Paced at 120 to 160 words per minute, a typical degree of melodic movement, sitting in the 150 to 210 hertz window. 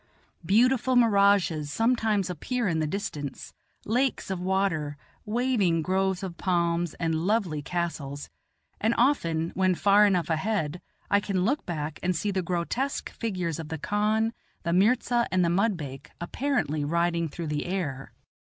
Yes: average, 145 wpm; average, 4.4 semitones; medium, 185 Hz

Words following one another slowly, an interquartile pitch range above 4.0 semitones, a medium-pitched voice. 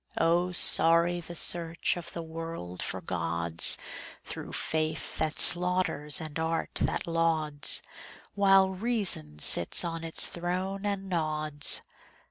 No: slow, 120 wpm; narrow, 2.6 semitones; medium, 165 Hz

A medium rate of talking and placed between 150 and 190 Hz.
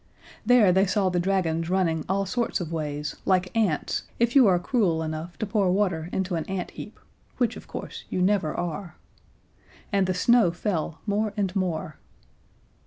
Yes: average, 175 wpm; medium, 185 Hz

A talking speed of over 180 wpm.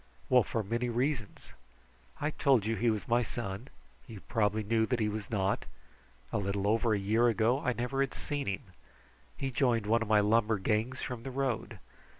Yes: average, 190 wpm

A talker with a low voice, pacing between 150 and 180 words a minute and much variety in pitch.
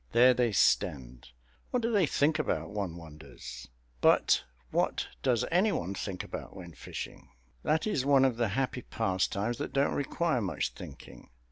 Yes: low, 120 Hz; average, 160 wpm; wide, 7.6 semitones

